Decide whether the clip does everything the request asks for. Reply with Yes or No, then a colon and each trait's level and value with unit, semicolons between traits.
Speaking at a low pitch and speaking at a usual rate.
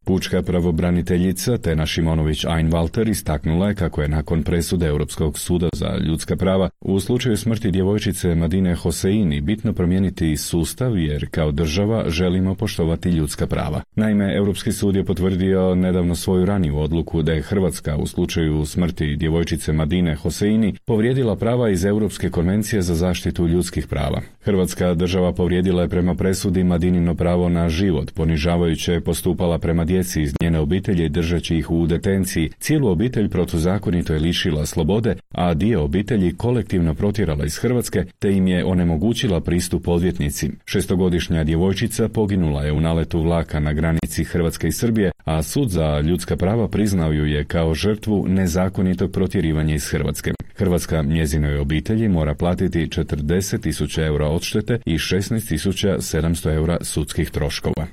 Yes: very low, 90 Hz; average, 145 wpm